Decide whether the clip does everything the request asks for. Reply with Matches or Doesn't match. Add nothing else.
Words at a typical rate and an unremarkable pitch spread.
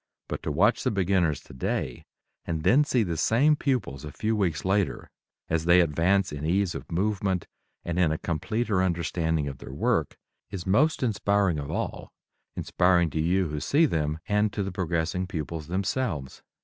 Matches